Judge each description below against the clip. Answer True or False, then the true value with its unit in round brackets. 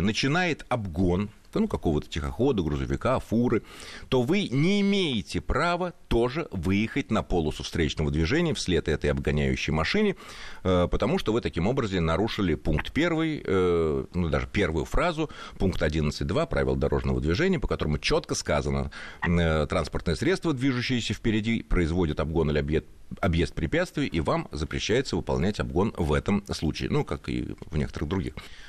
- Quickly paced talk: False (145 wpm)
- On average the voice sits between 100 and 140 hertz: False (90 Hz)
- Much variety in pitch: True (7.4 semitones)